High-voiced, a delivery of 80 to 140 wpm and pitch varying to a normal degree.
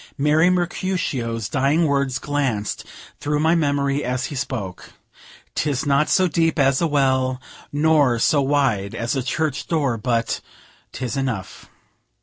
No: medium, 140 Hz; slow, 135 wpm; average, 3.0 semitones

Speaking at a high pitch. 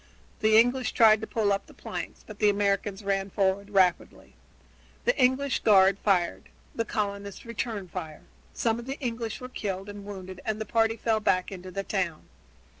Yes: high, 205 Hz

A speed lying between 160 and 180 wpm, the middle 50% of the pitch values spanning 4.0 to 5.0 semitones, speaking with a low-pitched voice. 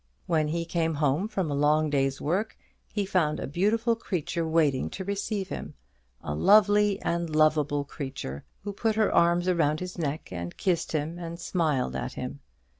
No: average, 175 wpm; average, 4.4 semitones; medium, 165 Hz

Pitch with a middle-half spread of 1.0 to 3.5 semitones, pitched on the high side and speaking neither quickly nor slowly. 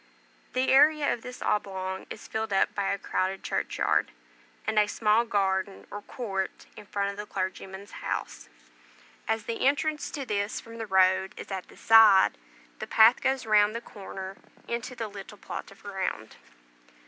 Yes: average, 2.9 semitones; high, 205 Hz; average, 170 wpm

